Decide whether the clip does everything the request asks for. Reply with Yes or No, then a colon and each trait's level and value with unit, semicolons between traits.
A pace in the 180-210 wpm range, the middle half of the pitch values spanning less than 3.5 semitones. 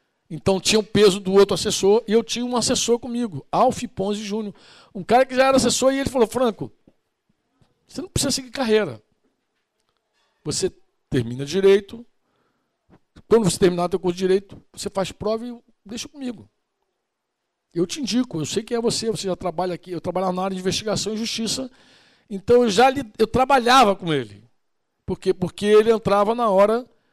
No: fast, 185 wpm; average, 4.2 semitones